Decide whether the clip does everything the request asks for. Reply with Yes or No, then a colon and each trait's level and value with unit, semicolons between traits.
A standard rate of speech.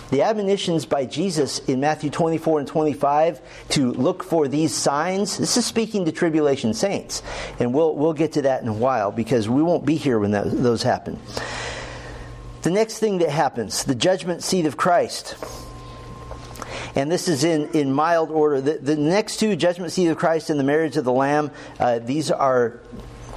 Yes: average, 185 wpm